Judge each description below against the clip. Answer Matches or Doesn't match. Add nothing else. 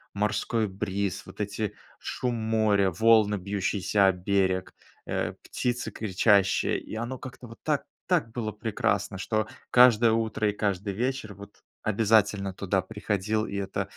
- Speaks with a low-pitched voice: Matches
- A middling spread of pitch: Doesn't match